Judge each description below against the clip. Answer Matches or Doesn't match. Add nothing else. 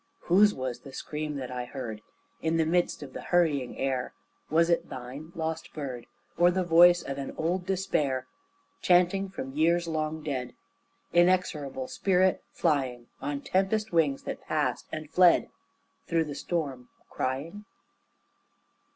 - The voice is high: Doesn't match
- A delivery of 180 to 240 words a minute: Doesn't match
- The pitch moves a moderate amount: Matches